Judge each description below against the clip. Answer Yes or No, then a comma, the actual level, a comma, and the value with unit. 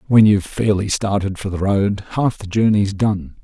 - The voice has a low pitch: Yes, low, 100 Hz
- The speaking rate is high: No, average, 190 wpm